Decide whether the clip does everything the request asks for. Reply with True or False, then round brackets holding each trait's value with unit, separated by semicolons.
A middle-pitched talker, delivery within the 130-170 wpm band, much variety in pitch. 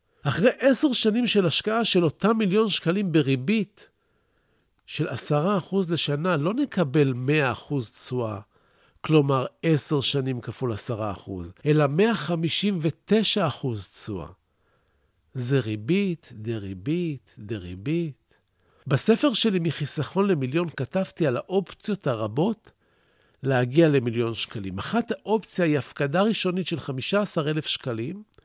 False (155 Hz; 120 wpm; 7.5 semitones)